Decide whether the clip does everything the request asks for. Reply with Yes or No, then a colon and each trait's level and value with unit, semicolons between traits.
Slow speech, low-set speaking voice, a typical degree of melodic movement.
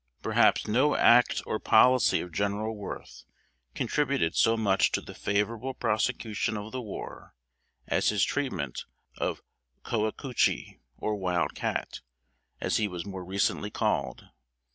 Yes: slow, 130 wpm; low, 105 Hz; average, 3.3 semitones